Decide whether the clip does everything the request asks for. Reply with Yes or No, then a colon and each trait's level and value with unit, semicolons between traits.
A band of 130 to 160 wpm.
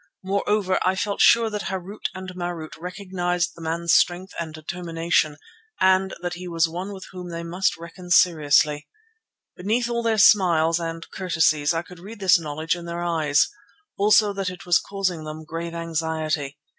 No: average, 170 wpm